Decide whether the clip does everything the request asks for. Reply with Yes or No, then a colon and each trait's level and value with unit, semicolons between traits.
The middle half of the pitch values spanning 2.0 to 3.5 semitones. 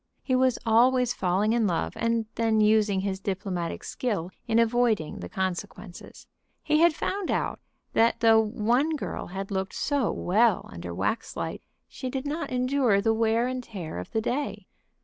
No: average, 4.3 semitones